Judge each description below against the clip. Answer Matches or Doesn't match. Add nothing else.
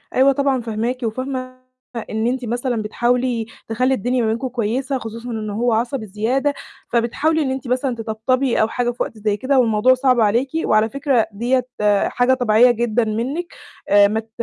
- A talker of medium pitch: Doesn't match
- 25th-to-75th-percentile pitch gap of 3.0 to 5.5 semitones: Doesn't match